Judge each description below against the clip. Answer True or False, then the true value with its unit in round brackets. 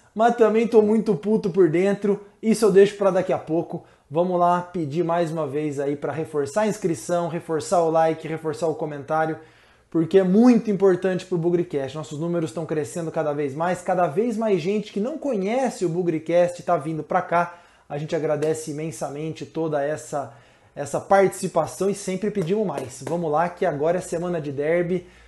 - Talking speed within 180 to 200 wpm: True (185 wpm)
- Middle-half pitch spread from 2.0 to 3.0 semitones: False (3.6 semitones)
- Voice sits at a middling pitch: True (170 Hz)